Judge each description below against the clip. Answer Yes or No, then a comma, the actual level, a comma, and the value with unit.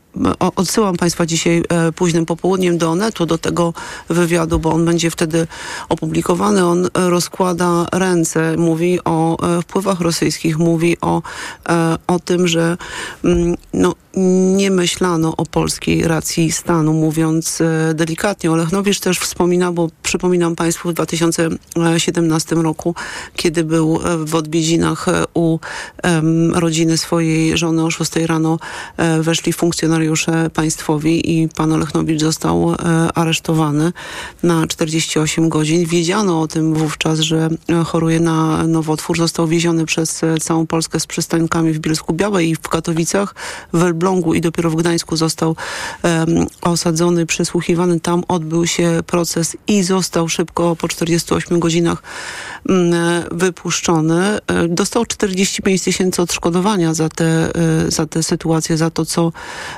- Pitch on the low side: No, medium, 165 Hz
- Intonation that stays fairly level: Yes, narrow, 1.3 semitones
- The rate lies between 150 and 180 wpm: No, average, 125 wpm